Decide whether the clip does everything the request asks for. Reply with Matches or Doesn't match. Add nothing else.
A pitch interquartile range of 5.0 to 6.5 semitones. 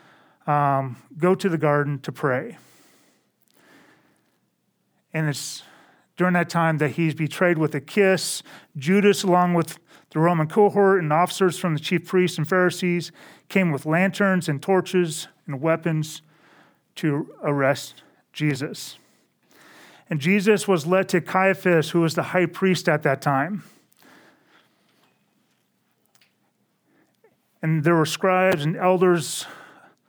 Doesn't match